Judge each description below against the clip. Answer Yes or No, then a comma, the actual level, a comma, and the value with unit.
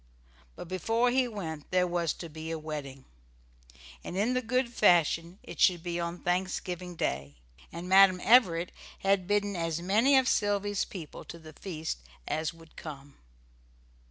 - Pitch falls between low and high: Yes, medium, 180 Hz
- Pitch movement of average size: Yes, average, 3.9 semitones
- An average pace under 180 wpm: Yes, average, 160 wpm